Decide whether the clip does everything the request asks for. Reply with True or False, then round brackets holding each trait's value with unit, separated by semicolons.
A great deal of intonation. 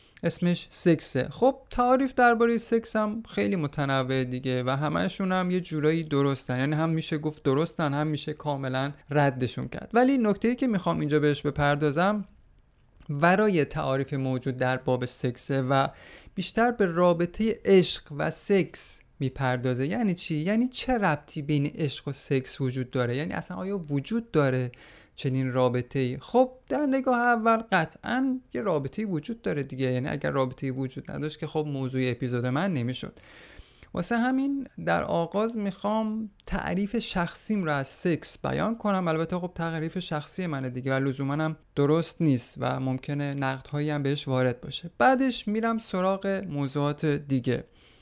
True (6.8 semitones)